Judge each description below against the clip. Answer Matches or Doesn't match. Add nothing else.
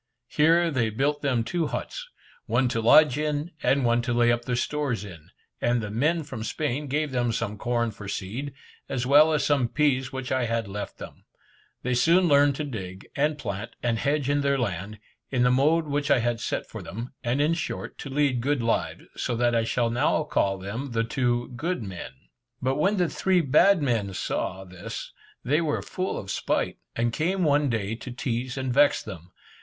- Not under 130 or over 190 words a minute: Doesn't match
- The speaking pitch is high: Doesn't match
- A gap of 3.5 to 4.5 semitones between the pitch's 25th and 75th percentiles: Matches